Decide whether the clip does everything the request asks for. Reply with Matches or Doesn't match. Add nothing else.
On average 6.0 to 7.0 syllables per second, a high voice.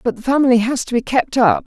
Matches